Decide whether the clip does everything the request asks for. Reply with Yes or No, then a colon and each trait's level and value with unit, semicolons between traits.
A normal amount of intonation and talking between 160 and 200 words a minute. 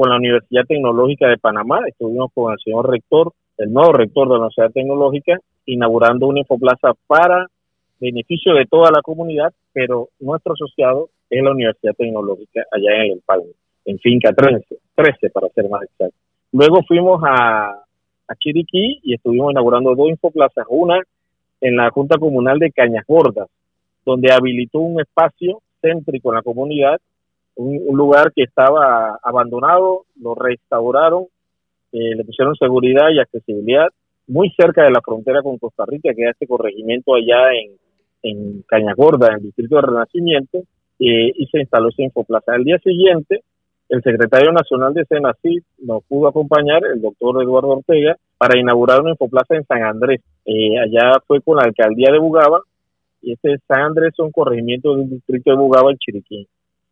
Yes: average, 5.0 semitones; average, 170 wpm